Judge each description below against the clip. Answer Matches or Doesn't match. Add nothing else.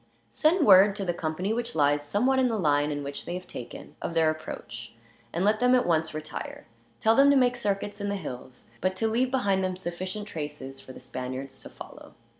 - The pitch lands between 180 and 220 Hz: Matches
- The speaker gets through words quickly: Matches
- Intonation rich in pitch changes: Matches